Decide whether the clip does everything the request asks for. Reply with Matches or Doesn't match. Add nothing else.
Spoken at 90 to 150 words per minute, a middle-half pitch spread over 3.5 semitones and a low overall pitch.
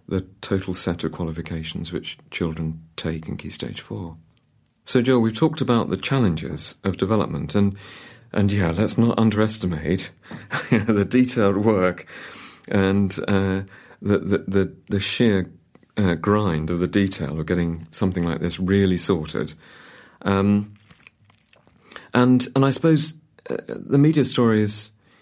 Matches